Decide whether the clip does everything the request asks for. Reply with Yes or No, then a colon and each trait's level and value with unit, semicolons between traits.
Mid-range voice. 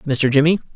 Yes: medium, 145 Hz